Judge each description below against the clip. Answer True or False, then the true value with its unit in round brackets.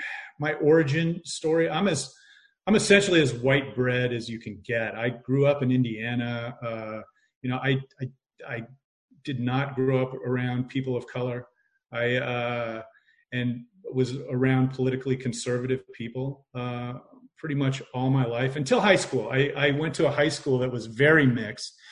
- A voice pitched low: True (130 Hz)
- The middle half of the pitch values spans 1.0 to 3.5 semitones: True (3.0 semitones)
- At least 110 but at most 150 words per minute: False (165 wpm)